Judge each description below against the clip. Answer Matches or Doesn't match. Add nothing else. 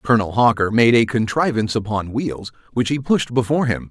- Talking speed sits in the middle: Matches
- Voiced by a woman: Doesn't match